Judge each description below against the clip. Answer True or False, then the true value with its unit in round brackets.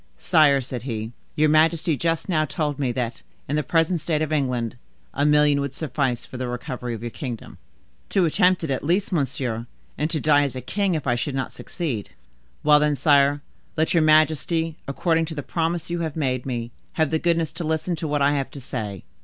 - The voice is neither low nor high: True (150 Hz)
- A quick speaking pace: True (210 wpm)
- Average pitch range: True (3.7 semitones)